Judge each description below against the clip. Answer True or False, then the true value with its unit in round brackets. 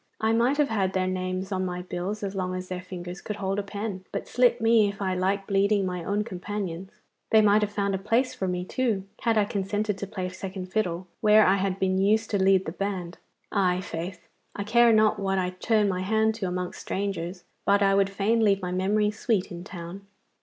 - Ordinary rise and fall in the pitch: False (2.3 semitones)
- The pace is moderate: False (225 wpm)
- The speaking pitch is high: True (195 Hz)